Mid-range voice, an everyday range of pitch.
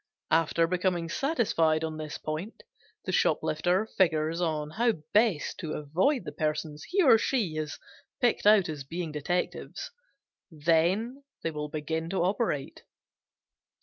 Yes: medium, 165 Hz; average, 5.0 semitones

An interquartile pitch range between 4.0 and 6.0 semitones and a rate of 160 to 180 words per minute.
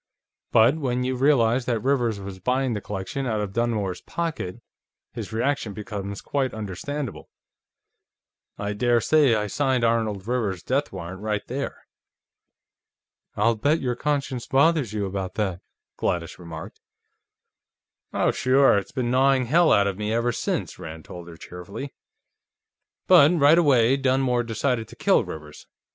No: average, 5.0 semitones; average, 145 wpm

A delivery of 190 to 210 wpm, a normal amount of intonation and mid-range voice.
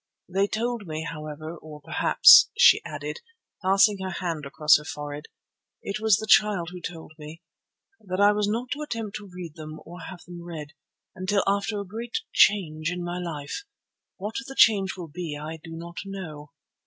No: average, 180 wpm; average, 4.4 semitones; medium, 180 Hz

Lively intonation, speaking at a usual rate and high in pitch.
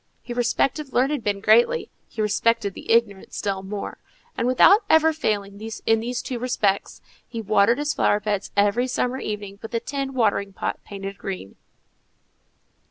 No: average, 3.8 semitones; average, 160 wpm; high, 225 Hz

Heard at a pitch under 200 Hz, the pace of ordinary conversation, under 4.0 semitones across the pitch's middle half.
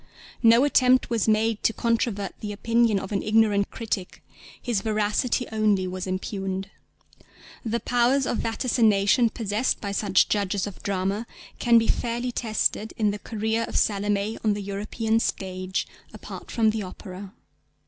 No: high, 215 Hz; average, 150 wpm; narrow, 2.4 semitones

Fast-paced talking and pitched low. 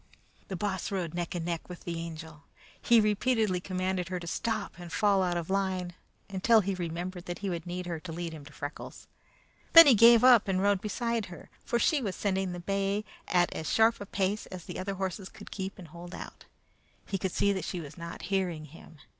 No: fast, 220 wpm; medium, 185 Hz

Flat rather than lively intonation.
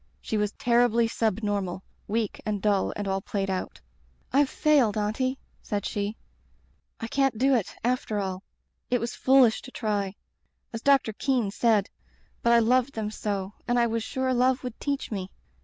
No: average, 3.5 semitones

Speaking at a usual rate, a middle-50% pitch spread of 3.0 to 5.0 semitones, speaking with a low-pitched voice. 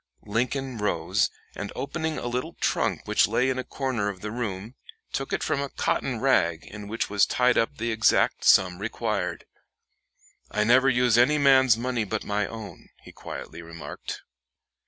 Yes: average, 170 wpm; average, 3.8 semitones; low, 115 Hz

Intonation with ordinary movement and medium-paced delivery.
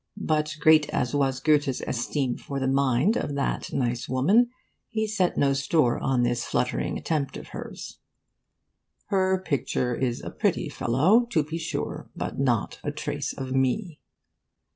Yes: average, 3.6 semitones; average, 155 wpm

